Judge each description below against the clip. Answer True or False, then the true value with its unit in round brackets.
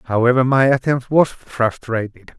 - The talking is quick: False (125 wpm)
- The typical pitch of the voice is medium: False (125 Hz)